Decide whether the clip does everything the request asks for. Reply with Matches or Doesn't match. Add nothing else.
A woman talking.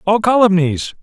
Doesn't match